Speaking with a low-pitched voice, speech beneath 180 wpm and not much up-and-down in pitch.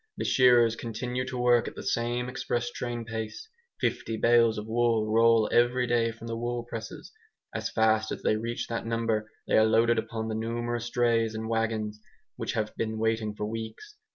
No: low, 115 Hz; average, 185 wpm; narrow, 1.3 semitones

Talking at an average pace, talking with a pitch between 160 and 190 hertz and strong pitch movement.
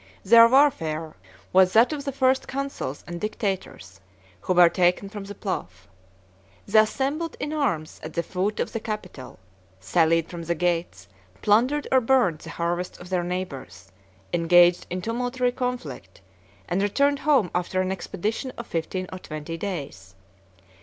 Yes: average, 155 wpm; medium, 185 Hz; wide, 6.3 semitones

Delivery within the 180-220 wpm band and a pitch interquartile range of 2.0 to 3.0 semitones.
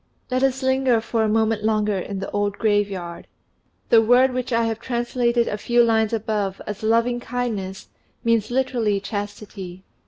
No: average, 160 wpm; average, 2.7 semitones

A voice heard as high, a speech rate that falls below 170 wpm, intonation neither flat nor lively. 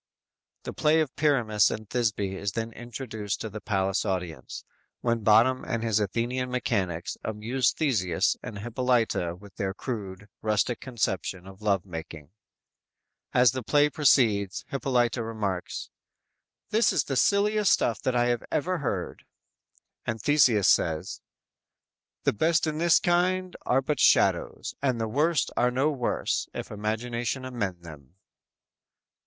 No: low, 115 Hz; average, 140 wpm; average, 4.5 semitones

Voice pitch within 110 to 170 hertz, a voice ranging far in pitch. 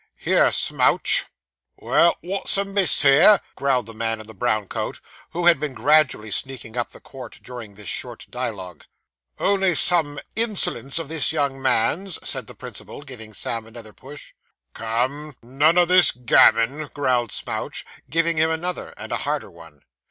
Yes: low, 135 Hz; wide, 6.1 semitones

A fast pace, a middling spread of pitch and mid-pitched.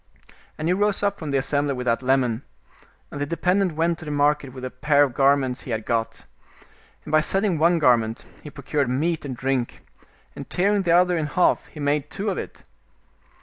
Yes: fast, 210 wpm; average, 4.5 semitones; medium, 145 Hz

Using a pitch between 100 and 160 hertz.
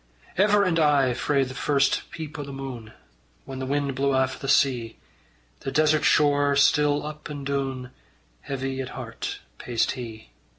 Yes: medium, 140 Hz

